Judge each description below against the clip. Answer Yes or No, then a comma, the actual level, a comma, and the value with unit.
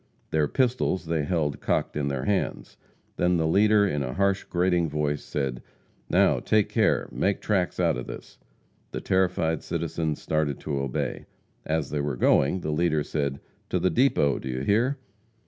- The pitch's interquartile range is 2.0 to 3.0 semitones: No, average, 4.5 semitones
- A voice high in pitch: No, very low, 80 Hz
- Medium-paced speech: Yes, average, 170 wpm